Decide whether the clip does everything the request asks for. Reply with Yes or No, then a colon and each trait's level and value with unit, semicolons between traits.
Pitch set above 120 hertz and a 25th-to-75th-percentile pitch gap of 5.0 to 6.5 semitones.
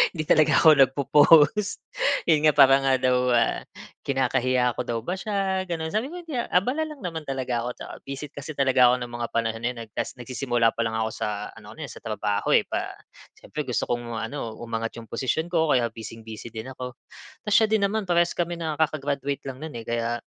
Yes: low, 135 Hz; wide, 5.5 semitones